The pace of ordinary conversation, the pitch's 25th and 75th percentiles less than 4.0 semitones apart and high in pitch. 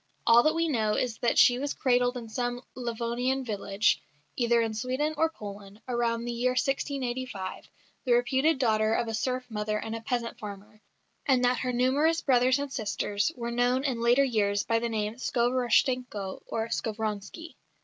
Yes: average, 170 wpm; narrow, 2.6 semitones; high, 240 Hz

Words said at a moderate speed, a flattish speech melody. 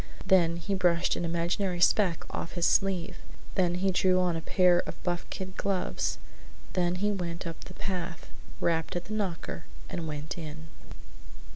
Yes: average, 165 wpm; narrow, 1.9 semitones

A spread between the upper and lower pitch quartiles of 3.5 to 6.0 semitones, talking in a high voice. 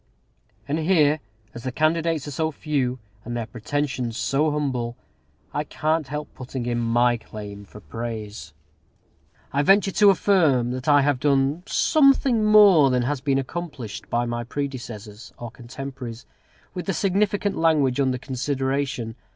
No: average, 4.6 semitones; low, 135 Hz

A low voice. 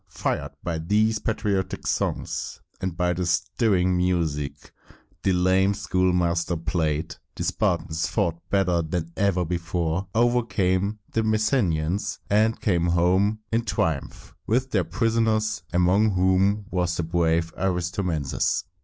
Yes: very low, 90 Hz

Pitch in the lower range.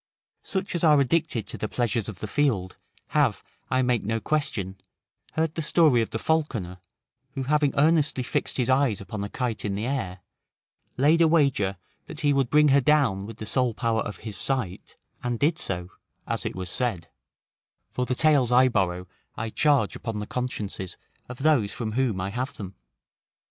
Yes: low, 125 Hz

